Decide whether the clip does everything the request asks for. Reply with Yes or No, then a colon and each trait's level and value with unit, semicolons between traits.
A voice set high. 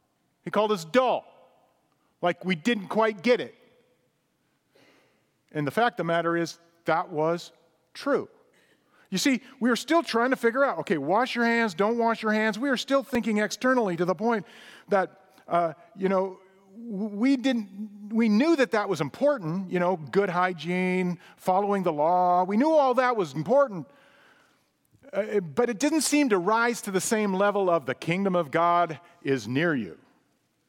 Yes: high, 205 Hz